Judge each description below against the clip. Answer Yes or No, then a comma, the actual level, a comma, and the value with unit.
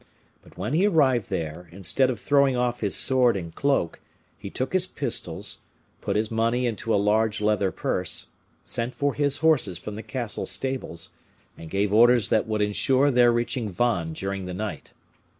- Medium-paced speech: Yes, average, 175 wpm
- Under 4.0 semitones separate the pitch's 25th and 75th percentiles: No, average, 4.5 semitones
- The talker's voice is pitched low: Yes, low, 115 Hz